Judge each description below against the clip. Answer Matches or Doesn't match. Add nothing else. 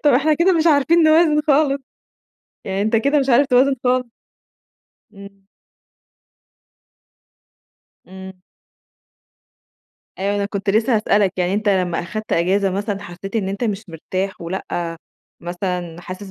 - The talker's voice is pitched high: Matches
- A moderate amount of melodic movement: Doesn't match